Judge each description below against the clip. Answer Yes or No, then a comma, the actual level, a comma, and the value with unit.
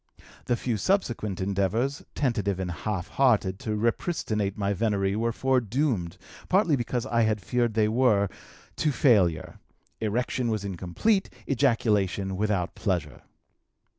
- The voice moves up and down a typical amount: Yes, average, 4.1 semitones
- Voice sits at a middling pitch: No, low, 110 Hz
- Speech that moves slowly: Yes, slow, 125 wpm